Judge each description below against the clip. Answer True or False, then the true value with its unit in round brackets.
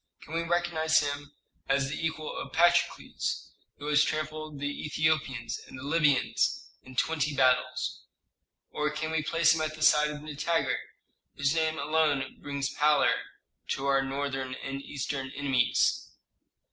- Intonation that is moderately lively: False (2.3 semitones)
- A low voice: False (150 Hz)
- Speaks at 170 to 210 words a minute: False (145 wpm)